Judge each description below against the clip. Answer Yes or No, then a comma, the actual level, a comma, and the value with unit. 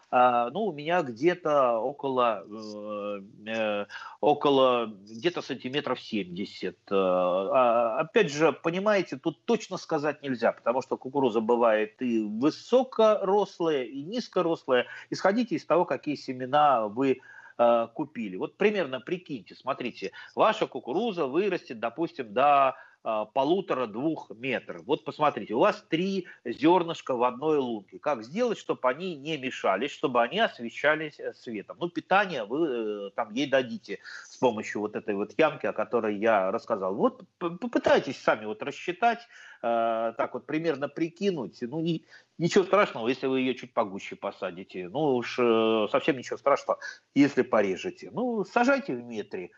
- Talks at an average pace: Yes, average, 135 wpm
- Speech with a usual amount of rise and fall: No, wide, 7.4 semitones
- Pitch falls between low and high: Yes, medium, 145 Hz